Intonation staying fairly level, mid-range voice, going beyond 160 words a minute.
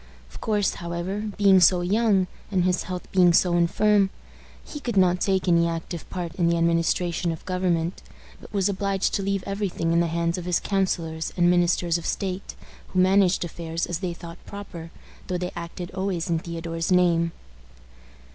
Yes: narrow, 2.2 semitones; medium, 180 Hz; average, 180 wpm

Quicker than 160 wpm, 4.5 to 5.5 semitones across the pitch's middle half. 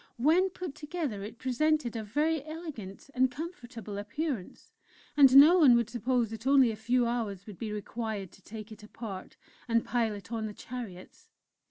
Yes: average, 175 wpm; average, 4.8 semitones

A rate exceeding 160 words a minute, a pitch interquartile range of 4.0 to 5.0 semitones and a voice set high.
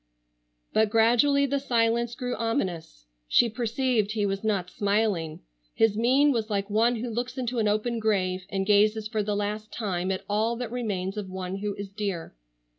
No: average, 180 wpm; average, 3.0 semitones; high, 215 Hz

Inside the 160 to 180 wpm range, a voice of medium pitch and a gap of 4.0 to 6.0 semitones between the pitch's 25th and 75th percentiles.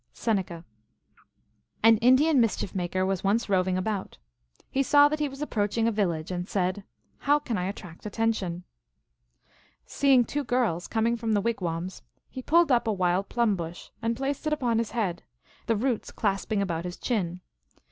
No: average, 175 wpm; high, 215 Hz; average, 4.9 semitones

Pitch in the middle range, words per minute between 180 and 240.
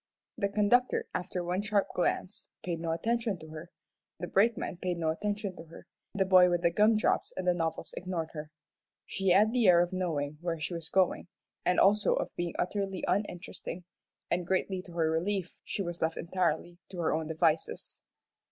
Yes: medium, 180 Hz; average, 185 wpm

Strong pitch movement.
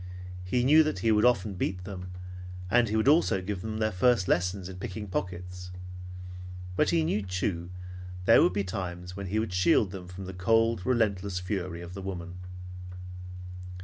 No: average, 3.2 semitones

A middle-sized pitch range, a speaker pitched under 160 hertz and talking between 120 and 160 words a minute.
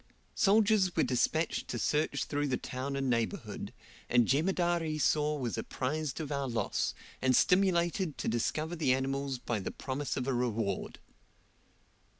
Yes: average, 4.1 semitones; medium, 140 Hz; average, 150 wpm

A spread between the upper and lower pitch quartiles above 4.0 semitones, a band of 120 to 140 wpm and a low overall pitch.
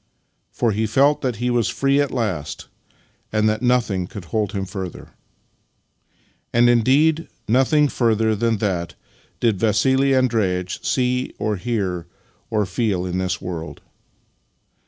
Yes: average, 4.6 semitones; slow, 135 wpm; low, 110 Hz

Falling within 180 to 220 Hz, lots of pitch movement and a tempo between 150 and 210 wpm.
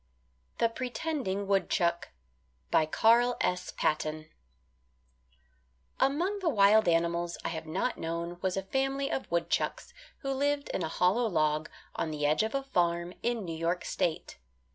No: high, 190 Hz; wide, 6.8 semitones; average, 140 wpm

